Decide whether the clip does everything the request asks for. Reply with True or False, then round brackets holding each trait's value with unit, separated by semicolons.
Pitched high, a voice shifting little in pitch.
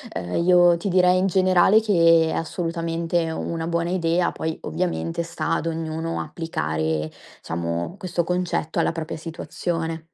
False (165 Hz; 1.5 semitones)